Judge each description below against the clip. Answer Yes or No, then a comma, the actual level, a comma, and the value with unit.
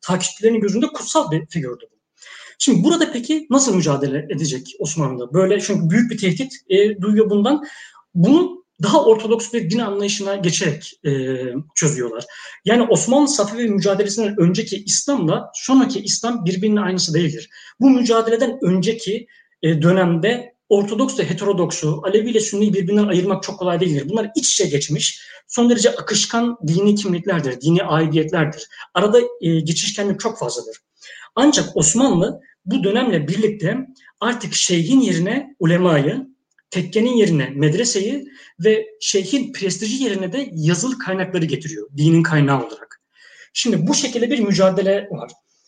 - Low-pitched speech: No, high, 200 Hz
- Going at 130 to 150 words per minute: Yes, average, 135 wpm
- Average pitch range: No, wide, 5.7 semitones